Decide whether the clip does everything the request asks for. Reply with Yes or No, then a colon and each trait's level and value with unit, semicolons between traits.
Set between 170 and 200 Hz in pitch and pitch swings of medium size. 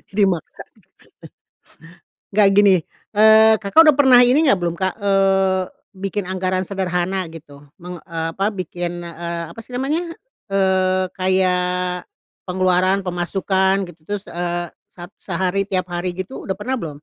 No: medium, 185 Hz; narrow, 2.0 semitones